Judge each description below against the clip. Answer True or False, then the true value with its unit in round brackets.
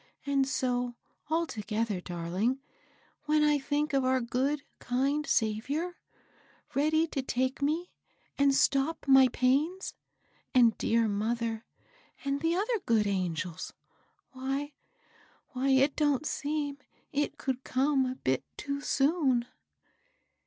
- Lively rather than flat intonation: False (3.5 semitones)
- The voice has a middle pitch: False (270 Hz)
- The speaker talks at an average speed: False (120 wpm)